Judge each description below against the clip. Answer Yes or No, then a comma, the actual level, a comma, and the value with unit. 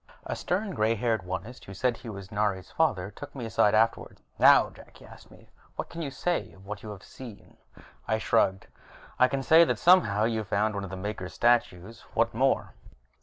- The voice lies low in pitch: Yes, low, 110 Hz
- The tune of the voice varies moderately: Yes, average, 4.3 semitones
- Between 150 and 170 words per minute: No, fast, 205 wpm